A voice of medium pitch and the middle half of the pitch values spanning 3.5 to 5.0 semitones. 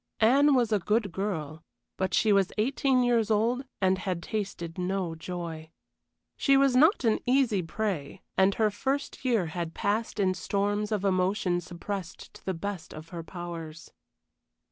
No: high, 195 Hz; average, 4.2 semitones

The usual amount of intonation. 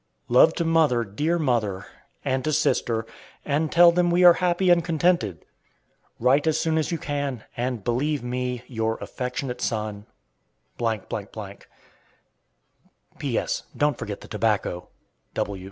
No: wide, 6.1 semitones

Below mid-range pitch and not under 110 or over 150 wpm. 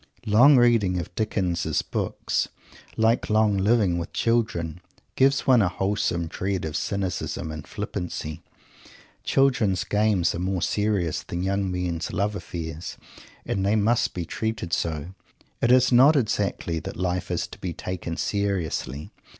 Yes: very low, 95 Hz; average, 140 wpm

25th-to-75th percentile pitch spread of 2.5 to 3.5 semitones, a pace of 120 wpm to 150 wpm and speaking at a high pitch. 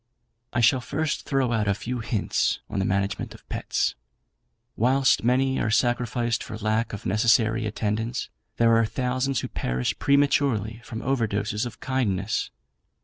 No: average, 2.9 semitones; average, 145 wpm; low, 115 Hz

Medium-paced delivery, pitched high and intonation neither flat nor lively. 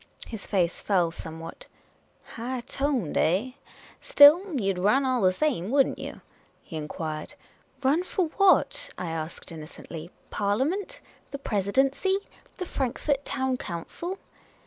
No: average, 145 wpm; high, 245 Hz; wide, 8.3 semitones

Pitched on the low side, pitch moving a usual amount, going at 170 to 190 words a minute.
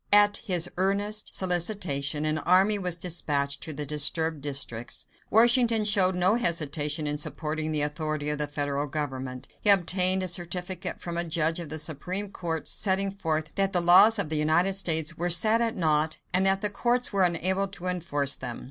No: medium, 170 Hz; average, 4.3 semitones; average, 185 wpm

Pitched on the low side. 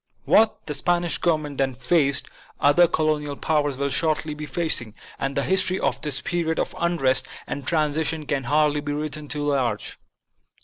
No: medium, 150 Hz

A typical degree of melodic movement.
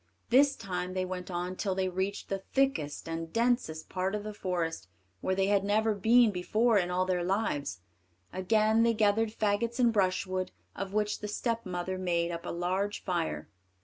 Yes: average, 3.1 semitones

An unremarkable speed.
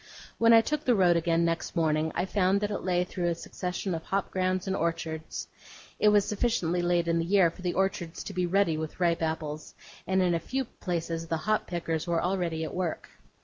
No: fast, 220 wpm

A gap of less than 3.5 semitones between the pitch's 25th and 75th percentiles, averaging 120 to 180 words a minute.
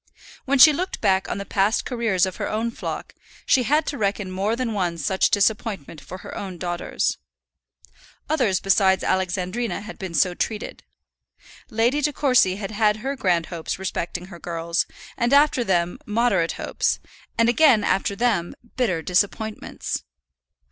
No: average, 4.5 semitones; average, 155 wpm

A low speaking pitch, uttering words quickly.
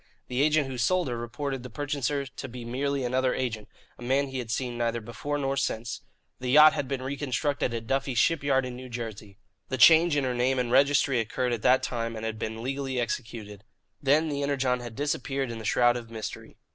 Yes: low, 130 Hz; fast, 210 wpm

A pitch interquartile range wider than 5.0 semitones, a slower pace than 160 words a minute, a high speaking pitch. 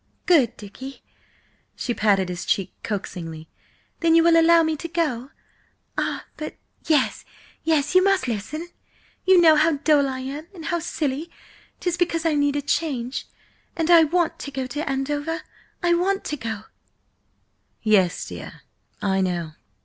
Yes: wide, 5.6 semitones; average, 150 wpm; very high, 295 Hz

